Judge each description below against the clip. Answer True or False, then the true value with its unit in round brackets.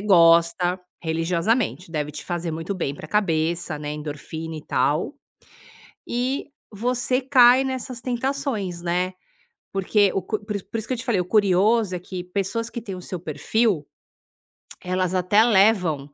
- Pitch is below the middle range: False (185 Hz)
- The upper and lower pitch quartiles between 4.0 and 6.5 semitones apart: True (5.2 semitones)